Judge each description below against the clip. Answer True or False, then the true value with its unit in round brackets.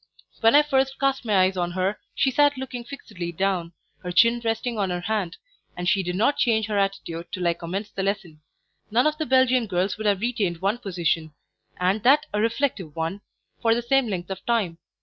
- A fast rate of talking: True (210 wpm)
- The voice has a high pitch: True (205 Hz)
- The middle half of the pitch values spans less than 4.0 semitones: False (5.0 semitones)